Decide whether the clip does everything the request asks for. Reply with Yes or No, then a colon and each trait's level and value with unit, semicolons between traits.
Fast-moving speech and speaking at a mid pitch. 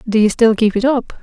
No: fast, 295 wpm; high, 225 Hz